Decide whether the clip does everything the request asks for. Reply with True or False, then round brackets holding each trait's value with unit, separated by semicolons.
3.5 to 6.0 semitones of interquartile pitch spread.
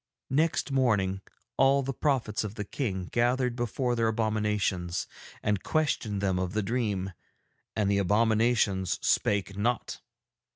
True (3.8 semitones)